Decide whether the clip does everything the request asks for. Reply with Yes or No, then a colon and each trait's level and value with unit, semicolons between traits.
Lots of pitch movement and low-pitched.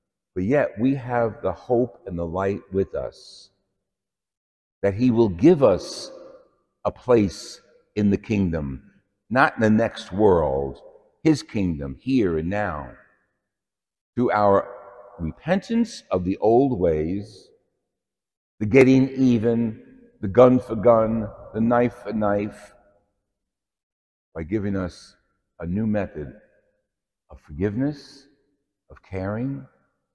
No: average, 4.3 semitones; low, 105 Hz